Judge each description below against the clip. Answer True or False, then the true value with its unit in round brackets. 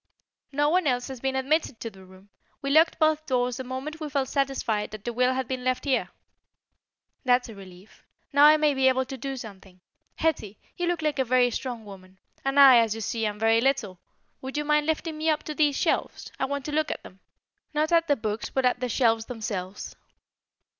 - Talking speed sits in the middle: False (220 wpm)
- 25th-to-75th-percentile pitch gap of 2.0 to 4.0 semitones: False (4.7 semitones)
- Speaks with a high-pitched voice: True (260 Hz)